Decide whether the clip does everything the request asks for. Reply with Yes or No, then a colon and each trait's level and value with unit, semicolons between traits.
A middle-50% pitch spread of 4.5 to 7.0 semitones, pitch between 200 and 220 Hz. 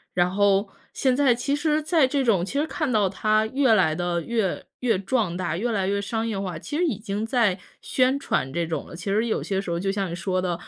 Yes: average, 5.2 semitones; high, 205 Hz